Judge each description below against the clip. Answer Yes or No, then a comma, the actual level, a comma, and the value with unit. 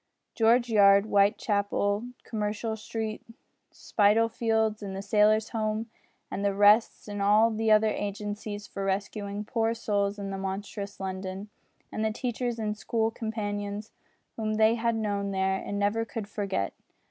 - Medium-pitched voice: No, high, 210 Hz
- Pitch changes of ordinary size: No, narrow, 1.6 semitones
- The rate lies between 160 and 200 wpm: No, average, 140 wpm